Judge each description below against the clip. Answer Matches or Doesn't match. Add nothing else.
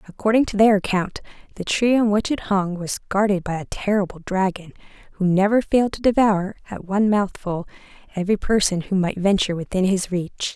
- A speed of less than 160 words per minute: Doesn't match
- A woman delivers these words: Matches